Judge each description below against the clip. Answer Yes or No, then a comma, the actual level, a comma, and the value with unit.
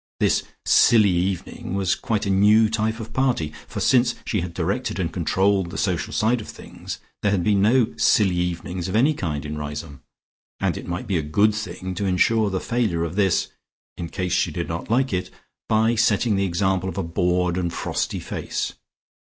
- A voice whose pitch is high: No, very low, 95 Hz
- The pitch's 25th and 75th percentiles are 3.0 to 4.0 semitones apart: Yes, average, 3.7 semitones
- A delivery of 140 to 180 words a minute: No, average, 195 wpm